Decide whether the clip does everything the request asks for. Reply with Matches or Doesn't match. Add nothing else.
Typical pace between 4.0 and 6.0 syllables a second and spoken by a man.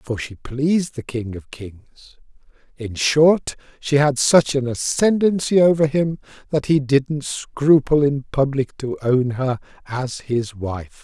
Doesn't match